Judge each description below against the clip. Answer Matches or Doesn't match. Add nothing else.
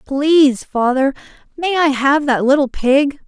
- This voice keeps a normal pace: Matches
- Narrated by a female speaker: Matches